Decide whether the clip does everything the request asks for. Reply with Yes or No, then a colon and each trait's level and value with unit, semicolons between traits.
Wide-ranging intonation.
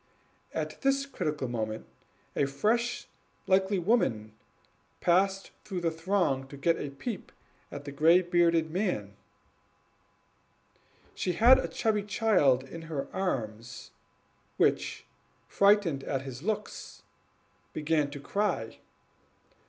Yes: wide, 6.6 semitones